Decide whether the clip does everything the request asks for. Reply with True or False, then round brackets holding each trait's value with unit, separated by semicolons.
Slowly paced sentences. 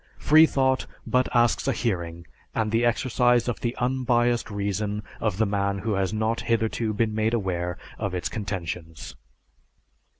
False (145 wpm)